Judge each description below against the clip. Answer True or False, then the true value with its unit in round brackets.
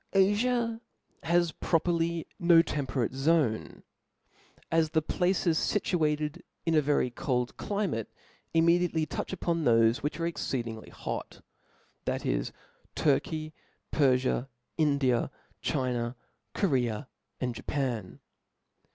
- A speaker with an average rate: False (100 wpm)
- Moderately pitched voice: True (155 Hz)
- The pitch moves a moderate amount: True (5.0 semitones)